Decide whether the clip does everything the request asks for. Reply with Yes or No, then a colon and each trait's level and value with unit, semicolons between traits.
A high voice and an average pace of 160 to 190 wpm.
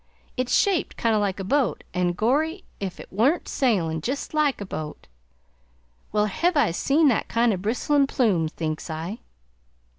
Yes: high, 220 Hz; average, 175 wpm